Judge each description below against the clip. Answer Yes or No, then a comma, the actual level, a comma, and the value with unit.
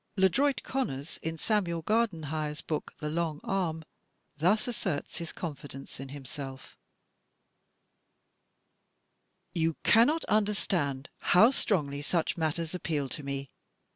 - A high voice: No, medium, 160 Hz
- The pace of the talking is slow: Yes, slow, 105 wpm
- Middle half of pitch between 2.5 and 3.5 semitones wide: No, average, 5.0 semitones